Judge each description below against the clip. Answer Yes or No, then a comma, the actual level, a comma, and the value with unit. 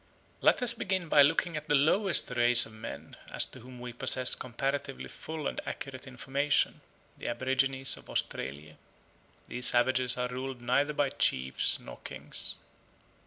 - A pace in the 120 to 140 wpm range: No, average, 155 wpm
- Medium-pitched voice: No, low, 130 Hz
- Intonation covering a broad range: No, average, 2.9 semitones